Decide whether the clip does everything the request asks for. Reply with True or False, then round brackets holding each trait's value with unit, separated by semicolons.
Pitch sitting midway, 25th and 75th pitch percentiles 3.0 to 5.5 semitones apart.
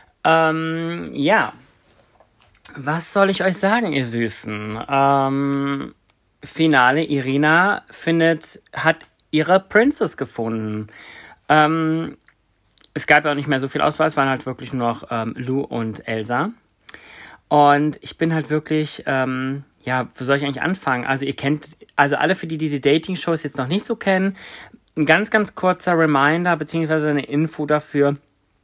True (150 Hz; 3.4 semitones)